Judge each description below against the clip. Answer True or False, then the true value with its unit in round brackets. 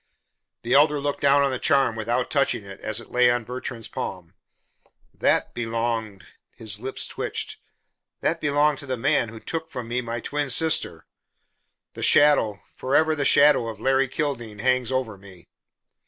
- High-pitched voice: False (125 Hz)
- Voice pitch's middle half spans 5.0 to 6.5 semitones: False (4.0 semitones)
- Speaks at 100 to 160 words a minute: False (170 wpm)